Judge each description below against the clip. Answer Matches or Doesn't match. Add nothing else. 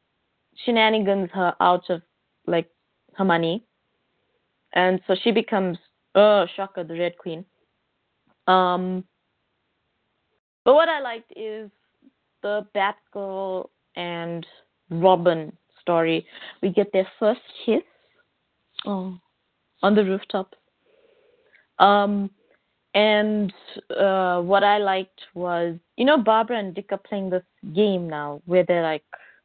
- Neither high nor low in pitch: Doesn't match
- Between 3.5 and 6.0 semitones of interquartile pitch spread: Doesn't match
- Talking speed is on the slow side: Matches